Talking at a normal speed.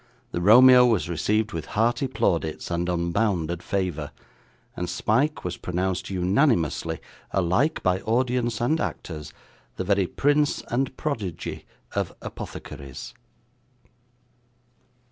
No: slow, 105 wpm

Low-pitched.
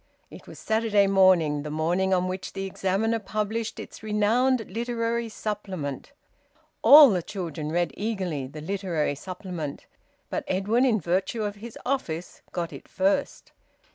No: high, 195 Hz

